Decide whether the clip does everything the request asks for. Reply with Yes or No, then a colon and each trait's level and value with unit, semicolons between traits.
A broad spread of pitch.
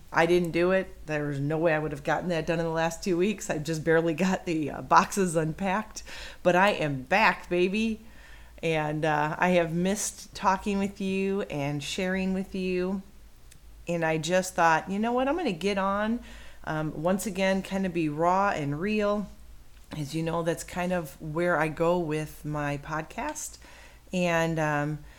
No: average, 3.4 semitones